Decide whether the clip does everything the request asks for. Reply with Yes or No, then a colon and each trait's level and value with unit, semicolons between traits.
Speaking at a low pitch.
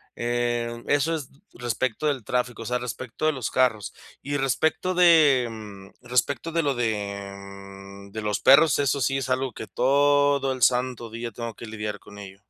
Yes: low, 120 Hz